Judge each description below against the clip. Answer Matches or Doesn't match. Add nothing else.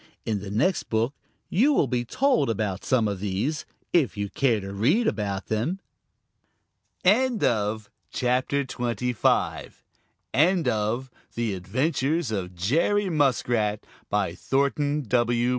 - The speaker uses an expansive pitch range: Matches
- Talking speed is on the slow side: Matches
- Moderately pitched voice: Doesn't match